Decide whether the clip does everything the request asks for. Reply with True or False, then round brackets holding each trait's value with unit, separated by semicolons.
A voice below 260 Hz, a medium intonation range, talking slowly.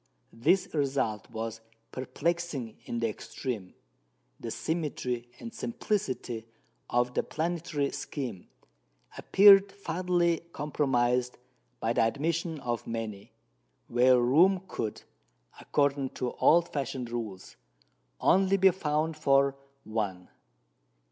False (135 Hz; 6.1 semitones; 100 wpm)